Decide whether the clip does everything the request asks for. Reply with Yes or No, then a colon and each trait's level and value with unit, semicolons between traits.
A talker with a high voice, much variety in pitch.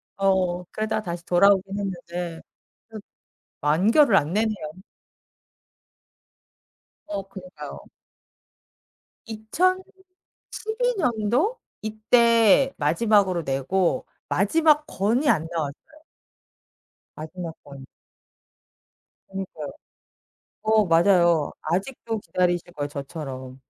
No: high, 195 Hz; average, 4.9 semitones